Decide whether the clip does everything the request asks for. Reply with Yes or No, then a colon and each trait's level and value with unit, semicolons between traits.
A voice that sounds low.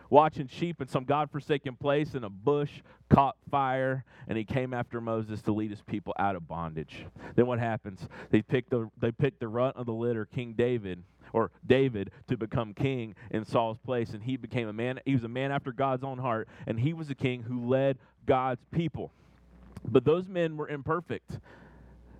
Yes: low, 125 Hz